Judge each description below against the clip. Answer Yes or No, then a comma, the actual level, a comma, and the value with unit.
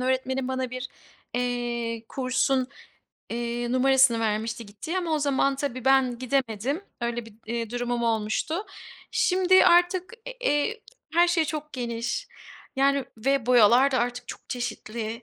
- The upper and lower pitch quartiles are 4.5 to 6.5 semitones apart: No, average, 3.0 semitones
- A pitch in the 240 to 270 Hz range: Yes, very high, 255 Hz